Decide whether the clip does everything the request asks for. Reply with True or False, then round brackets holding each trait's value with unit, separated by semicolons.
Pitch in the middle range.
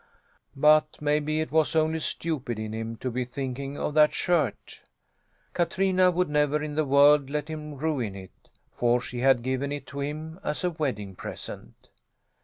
True (145 Hz)